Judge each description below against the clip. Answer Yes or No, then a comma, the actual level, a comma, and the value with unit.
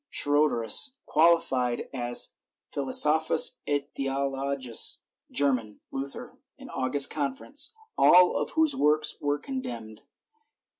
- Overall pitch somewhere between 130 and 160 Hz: Yes, medium, 140 Hz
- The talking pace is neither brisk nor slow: No, slow, 90 wpm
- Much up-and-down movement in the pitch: No, average, 3.2 semitones